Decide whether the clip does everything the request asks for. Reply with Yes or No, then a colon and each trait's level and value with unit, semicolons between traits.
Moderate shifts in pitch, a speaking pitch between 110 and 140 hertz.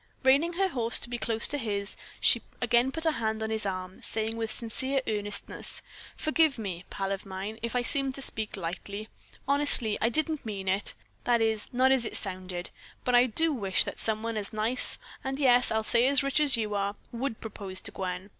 No: average, 4.4 semitones; high, 225 Hz